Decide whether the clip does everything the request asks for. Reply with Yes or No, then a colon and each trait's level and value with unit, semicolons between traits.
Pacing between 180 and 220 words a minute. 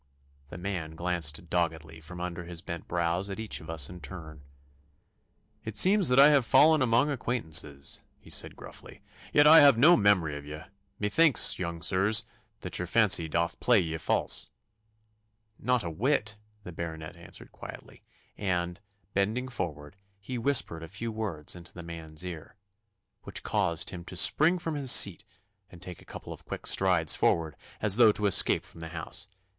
No: average, 170 wpm